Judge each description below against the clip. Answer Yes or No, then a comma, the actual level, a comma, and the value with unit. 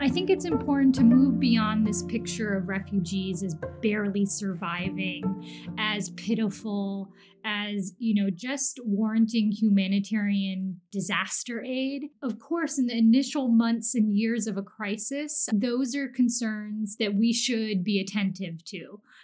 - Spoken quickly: No, slow, 135 wpm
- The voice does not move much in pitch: No, average, 3.2 semitones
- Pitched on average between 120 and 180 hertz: No, high, 215 Hz